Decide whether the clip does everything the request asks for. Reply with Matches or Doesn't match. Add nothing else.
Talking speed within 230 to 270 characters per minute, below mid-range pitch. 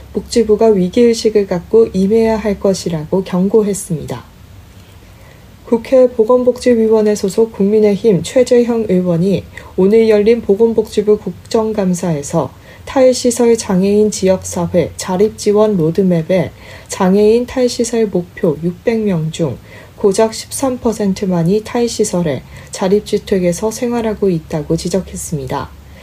Doesn't match